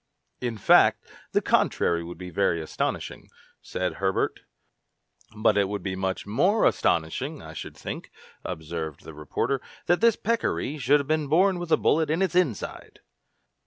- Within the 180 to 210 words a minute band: No, average, 160 wpm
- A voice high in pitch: No, low, 110 Hz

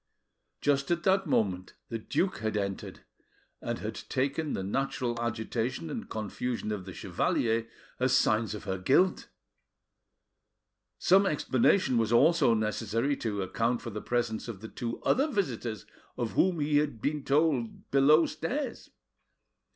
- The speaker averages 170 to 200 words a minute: No, average, 145 wpm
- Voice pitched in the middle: No, low, 120 Hz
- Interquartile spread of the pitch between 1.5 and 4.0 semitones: No, wide, 5.4 semitones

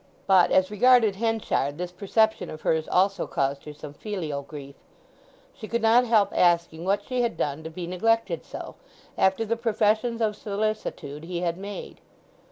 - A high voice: Yes, high, 195 Hz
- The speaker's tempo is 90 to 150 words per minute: No, average, 170 wpm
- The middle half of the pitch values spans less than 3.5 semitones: No, average, 5.1 semitones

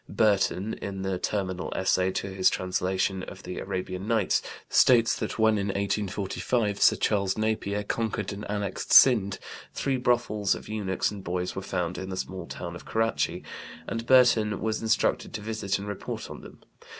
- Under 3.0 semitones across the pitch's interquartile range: Yes, narrow, 2.6 semitones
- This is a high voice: No, low, 100 Hz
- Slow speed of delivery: No, average, 170 wpm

